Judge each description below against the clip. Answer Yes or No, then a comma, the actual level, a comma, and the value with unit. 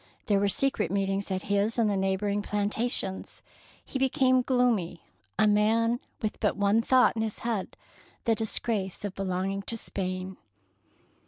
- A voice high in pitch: Yes, high, 205 Hz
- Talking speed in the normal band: Yes, average, 160 wpm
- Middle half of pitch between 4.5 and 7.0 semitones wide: No, average, 2.9 semitones